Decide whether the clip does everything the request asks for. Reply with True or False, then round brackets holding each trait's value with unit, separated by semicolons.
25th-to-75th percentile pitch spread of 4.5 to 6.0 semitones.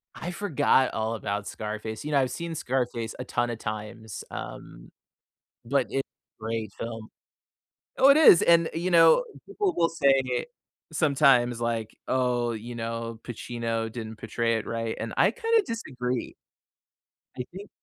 True (5.0 semitones)